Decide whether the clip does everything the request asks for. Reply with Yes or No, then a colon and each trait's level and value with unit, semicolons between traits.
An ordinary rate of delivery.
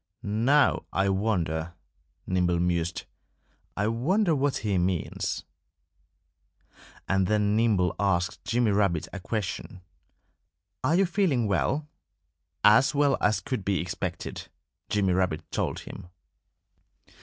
No: slow, 115 wpm